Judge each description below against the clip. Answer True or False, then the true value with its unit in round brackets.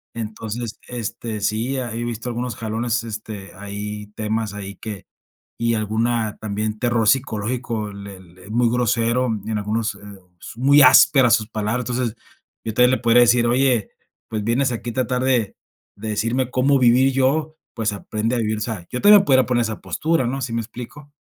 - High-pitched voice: False (115 Hz)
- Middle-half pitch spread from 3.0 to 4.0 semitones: False (2.6 semitones)